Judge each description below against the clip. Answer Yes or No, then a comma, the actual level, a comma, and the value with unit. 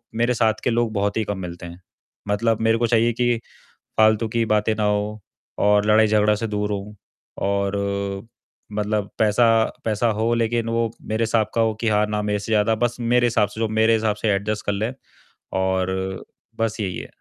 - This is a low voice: Yes, low, 110 Hz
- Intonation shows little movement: Yes, narrow, 1.7 semitones